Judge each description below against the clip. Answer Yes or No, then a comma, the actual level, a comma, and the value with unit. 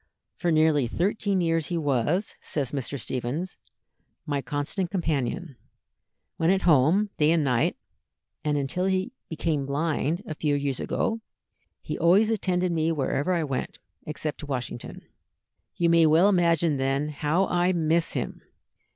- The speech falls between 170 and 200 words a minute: No, average, 145 wpm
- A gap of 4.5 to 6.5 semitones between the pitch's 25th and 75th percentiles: No, average, 3.8 semitones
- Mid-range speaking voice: Yes, medium, 160 Hz